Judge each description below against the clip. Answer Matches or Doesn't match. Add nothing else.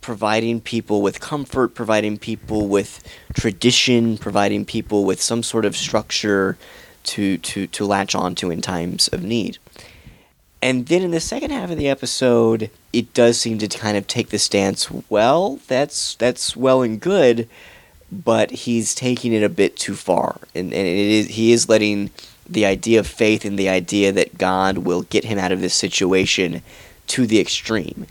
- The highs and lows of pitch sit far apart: Doesn't match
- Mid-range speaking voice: Doesn't match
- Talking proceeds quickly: Doesn't match